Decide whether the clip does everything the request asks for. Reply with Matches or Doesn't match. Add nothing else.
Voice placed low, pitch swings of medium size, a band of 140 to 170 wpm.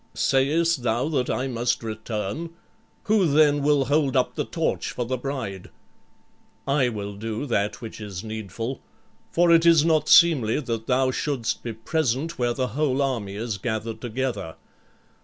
Matches